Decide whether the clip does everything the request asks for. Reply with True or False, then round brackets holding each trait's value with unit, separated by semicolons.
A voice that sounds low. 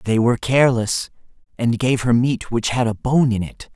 True (120 Hz)